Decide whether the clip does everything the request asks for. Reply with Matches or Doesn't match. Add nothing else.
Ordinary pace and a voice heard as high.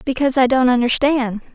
Matches